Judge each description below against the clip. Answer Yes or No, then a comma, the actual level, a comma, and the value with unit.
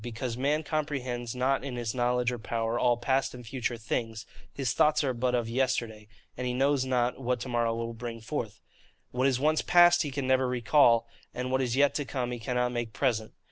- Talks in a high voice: No, low, 125 Hz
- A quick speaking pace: Yes, fast, 215 wpm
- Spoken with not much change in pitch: Yes, narrow, 2.1 semitones